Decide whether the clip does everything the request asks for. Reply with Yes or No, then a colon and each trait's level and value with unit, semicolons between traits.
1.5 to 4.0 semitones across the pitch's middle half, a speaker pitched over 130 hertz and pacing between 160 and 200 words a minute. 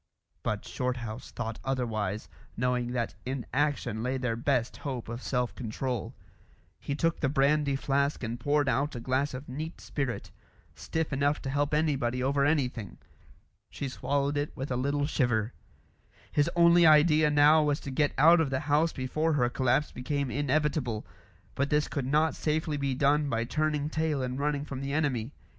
Yes: average, 2.9 semitones; medium, 140 Hz; average, 170 wpm